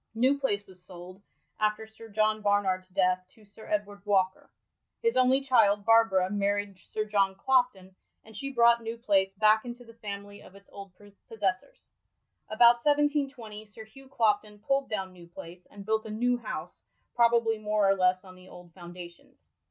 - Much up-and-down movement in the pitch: No, average, 3.2 semitones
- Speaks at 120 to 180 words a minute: Yes, average, 170 wpm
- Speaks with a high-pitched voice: Yes, high, 210 Hz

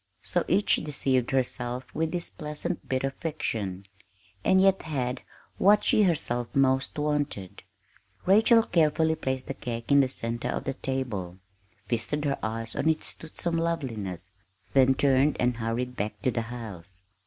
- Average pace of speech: Yes, average, 155 wpm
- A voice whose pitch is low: Yes, low, 130 Hz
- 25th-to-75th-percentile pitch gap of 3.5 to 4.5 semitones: No, average, 5.0 semitones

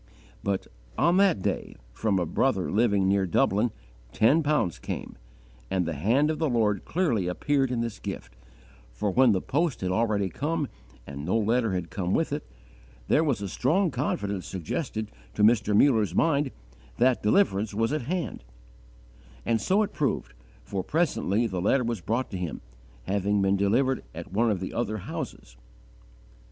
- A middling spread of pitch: No, wide, 5.8 semitones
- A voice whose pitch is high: No, low, 110 Hz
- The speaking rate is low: No, average, 165 wpm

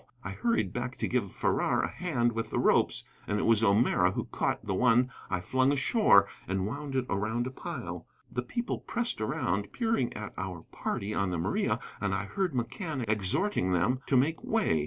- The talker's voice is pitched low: Yes, low, 120 Hz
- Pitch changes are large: Yes, wide, 5.9 semitones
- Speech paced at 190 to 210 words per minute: Yes, average, 195 wpm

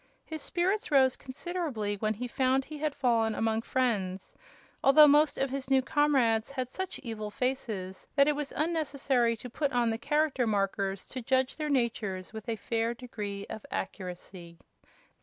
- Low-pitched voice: No, very high, 250 Hz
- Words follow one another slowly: No, average, 165 wpm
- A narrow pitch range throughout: No, average, 4.4 semitones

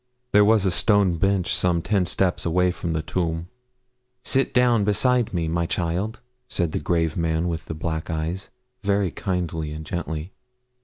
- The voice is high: No, very low, 90 Hz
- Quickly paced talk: No, average, 165 wpm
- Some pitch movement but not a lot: Yes, average, 3.4 semitones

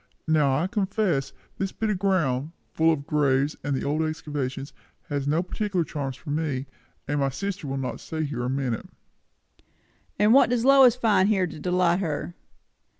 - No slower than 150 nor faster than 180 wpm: Yes, average, 170 wpm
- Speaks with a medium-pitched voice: Yes, medium, 155 Hz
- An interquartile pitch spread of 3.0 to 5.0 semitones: No, wide, 5.4 semitones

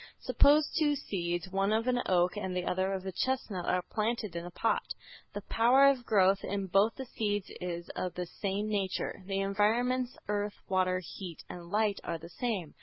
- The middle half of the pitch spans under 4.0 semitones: Yes, average, 3.6 semitones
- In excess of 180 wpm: Yes, average, 190 wpm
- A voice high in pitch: Yes, high, 195 Hz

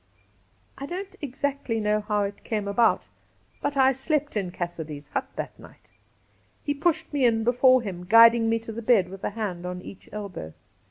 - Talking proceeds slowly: No, average, 180 wpm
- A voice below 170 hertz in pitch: No, high, 225 Hz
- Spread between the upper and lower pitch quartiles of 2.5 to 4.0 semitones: No, average, 5.1 semitones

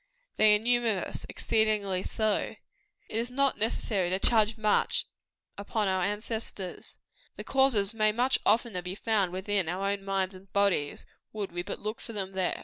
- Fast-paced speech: No, average, 165 wpm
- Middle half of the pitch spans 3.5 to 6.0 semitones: No, average, 2.7 semitones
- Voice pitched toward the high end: Yes, high, 205 Hz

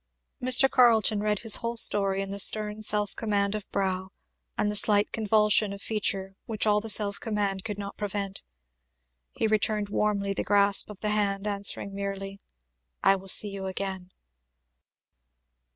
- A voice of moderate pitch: No, high, 205 Hz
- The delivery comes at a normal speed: Yes, average, 160 wpm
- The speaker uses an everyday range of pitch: No, narrow, 1.3 semitones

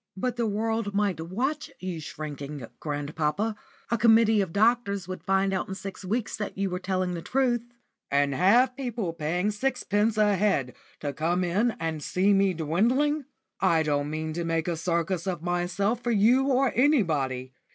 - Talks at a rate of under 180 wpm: Yes, average, 170 wpm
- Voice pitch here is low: No, high, 190 Hz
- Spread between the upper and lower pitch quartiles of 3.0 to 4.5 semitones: No, wide, 5.4 semitones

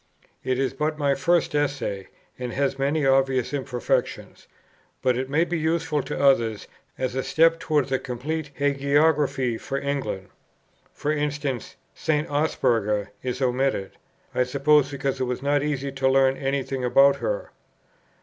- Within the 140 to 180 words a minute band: Yes, average, 150 wpm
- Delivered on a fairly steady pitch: Yes, narrow, 2.3 semitones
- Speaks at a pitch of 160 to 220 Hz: No, low, 135 Hz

